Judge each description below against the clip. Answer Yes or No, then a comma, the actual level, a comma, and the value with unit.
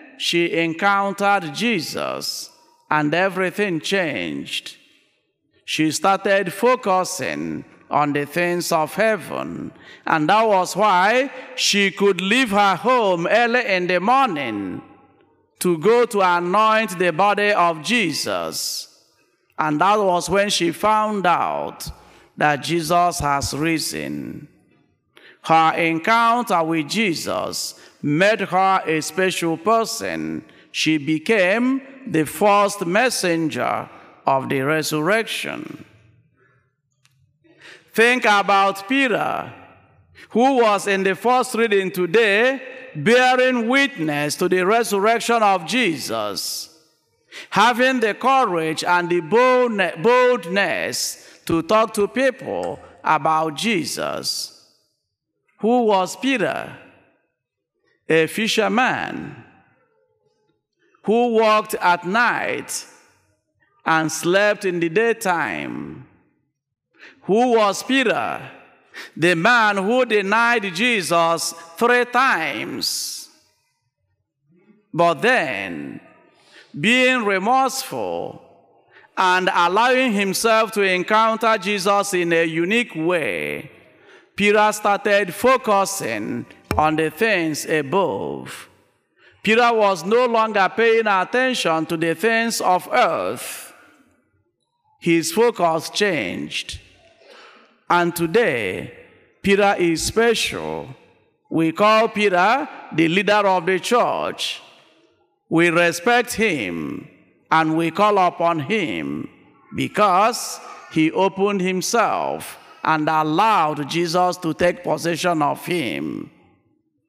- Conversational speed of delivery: No, slow, 95 wpm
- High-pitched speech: Yes, high, 200 Hz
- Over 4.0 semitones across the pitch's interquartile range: Yes, wide, 5.4 semitones